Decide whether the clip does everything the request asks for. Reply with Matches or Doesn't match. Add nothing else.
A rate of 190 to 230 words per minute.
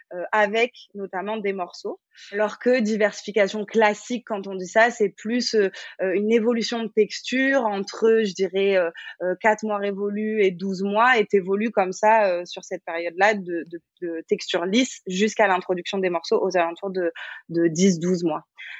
Doesn't match